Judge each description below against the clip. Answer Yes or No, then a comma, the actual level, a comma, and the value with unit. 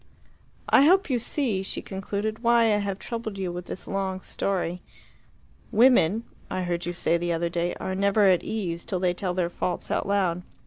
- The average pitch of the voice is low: No, high, 190 Hz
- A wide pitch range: No, average, 3.5 semitones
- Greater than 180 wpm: Yes, average, 190 wpm